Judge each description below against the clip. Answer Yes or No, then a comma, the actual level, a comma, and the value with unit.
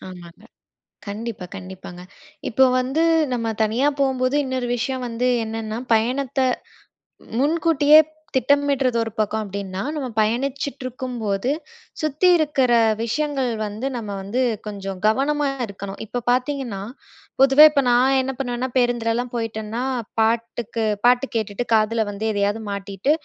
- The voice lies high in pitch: Yes, high, 240 Hz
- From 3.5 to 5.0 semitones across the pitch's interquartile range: Yes, average, 3.8 semitones